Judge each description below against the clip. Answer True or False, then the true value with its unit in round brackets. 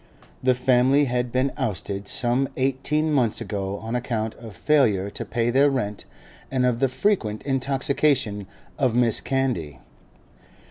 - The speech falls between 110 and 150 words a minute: True (140 wpm)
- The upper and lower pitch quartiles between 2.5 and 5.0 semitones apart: True (3.6 semitones)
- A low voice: True (125 Hz)